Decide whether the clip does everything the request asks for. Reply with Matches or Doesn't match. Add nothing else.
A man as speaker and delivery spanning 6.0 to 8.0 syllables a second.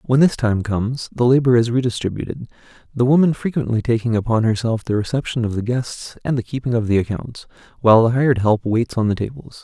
Matches